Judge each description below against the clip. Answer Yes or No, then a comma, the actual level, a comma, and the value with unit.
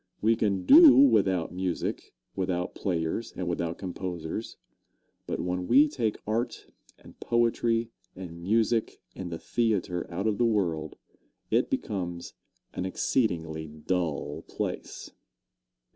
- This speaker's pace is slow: Yes, slow, 120 wpm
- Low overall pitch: Yes, very low, 95 Hz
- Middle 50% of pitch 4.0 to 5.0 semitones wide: Yes, average, 4.7 semitones